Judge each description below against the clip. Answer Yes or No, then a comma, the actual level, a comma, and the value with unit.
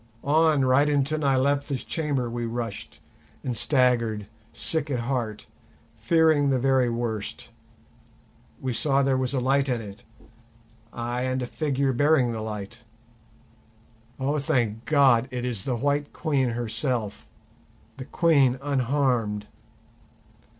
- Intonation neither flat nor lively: Yes, average, 3.2 semitones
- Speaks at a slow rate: Yes, slow, 125 wpm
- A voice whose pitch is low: Yes, low, 130 Hz